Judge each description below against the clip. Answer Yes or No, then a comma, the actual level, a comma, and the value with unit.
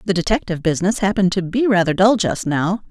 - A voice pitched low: No, high, 190 Hz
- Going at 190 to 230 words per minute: Yes, fast, 205 wpm